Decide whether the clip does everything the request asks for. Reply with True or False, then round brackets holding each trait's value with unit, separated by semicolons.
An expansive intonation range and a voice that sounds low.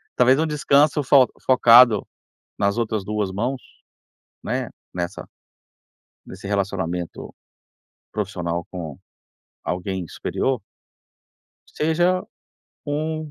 True (6.8 semitones; 110 Hz)